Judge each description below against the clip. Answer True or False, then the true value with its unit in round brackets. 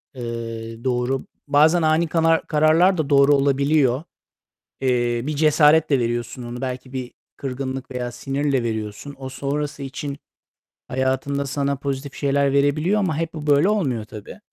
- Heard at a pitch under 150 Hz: True (140 Hz)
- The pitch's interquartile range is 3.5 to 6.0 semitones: False (2.9 semitones)